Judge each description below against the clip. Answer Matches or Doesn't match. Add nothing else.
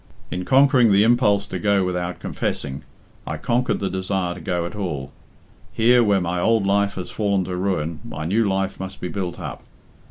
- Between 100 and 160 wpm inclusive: Doesn't match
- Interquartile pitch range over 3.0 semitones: Doesn't match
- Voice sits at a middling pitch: Doesn't match